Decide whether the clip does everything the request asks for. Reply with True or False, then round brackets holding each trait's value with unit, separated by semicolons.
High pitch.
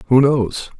False (130 Hz)